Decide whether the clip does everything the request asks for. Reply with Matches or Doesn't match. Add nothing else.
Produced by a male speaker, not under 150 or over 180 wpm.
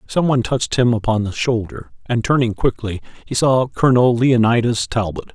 Matches